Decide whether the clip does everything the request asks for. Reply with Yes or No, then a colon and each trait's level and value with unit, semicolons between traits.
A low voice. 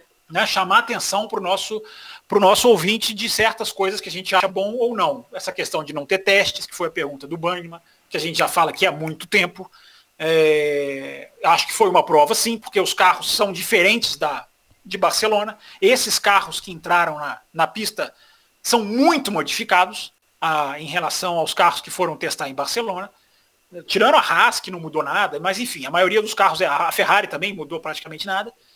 No: high, 190 Hz